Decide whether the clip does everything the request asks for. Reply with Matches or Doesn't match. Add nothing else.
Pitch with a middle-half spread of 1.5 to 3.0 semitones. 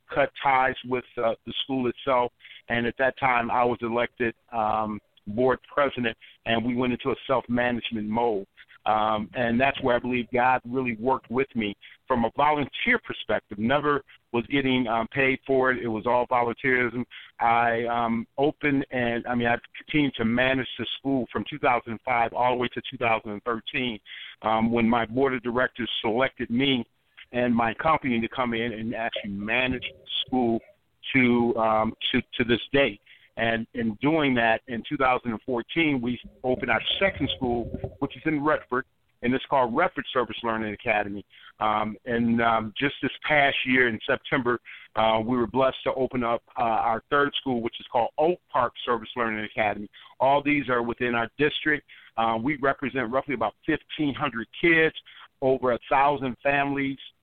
Matches